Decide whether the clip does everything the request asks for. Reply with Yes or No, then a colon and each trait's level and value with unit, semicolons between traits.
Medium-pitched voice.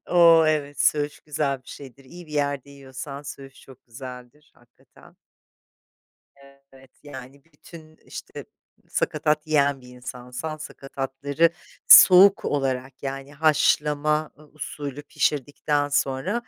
Yes: medium, 145 Hz